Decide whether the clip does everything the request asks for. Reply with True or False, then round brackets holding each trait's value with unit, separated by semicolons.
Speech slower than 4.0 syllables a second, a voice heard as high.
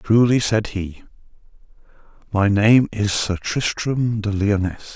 False (3.6 syllables/s; 105 Hz)